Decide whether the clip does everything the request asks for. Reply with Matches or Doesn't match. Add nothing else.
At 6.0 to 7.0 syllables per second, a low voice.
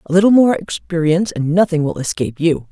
Doesn't match